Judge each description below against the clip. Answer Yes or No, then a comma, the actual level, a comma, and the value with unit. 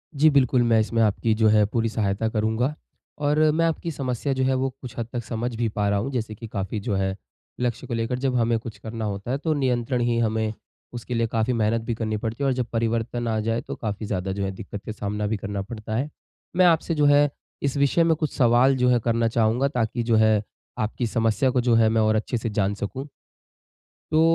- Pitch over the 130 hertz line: No, low, 115 Hz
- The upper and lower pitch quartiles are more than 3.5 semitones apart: No, average, 2.8 semitones